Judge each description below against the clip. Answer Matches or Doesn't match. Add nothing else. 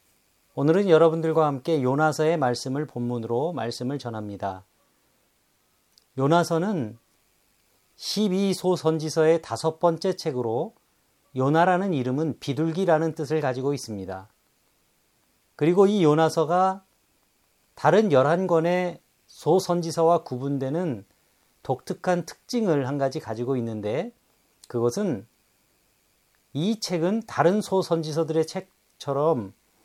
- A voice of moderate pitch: Matches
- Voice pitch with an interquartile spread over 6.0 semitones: Doesn't match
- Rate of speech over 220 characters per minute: Matches